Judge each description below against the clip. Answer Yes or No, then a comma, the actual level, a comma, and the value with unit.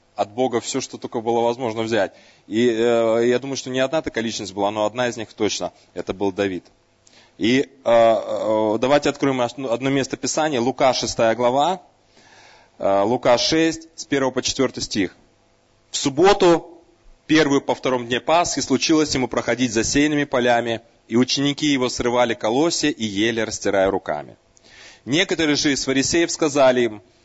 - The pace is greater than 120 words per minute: Yes, fast, 160 wpm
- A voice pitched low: Yes, low, 125 Hz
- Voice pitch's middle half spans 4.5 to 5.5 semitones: No, average, 3.7 semitones